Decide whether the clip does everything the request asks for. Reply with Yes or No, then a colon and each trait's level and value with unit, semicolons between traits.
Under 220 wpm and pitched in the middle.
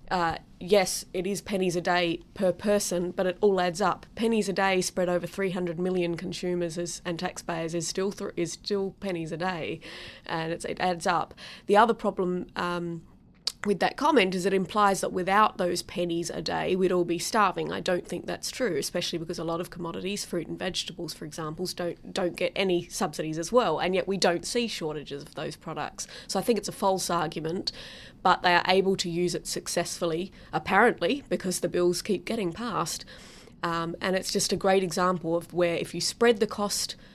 Yes: fast, 205 wpm; medium, 180 Hz